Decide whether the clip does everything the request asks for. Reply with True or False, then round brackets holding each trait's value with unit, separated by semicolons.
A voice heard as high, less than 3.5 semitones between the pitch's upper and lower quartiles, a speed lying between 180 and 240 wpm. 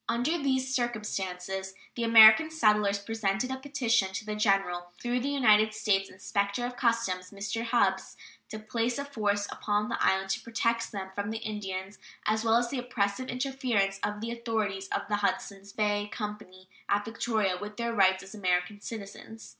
False (210 Hz; 3.0 semitones; 170 wpm)